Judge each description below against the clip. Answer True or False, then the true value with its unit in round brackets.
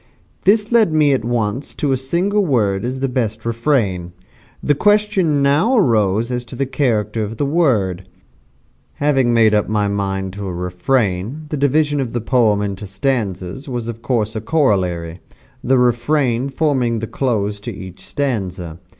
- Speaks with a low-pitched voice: True (120 Hz)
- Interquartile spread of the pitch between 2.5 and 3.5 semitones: False (5.6 semitones)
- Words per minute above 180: False (165 wpm)